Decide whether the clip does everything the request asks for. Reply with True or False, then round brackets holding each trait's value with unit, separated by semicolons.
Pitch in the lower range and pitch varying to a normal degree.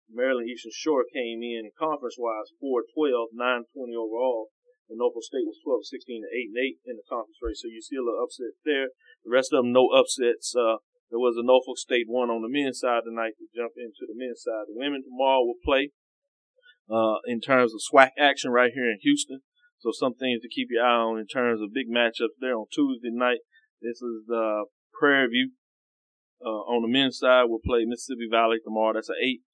True (125 Hz; 3.8 semitones)